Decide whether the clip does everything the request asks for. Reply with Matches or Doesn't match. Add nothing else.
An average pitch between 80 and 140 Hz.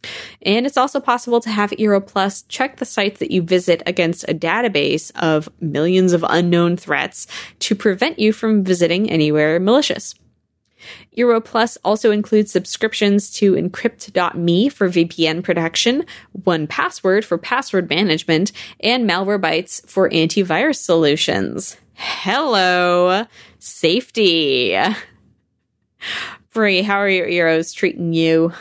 Doesn't match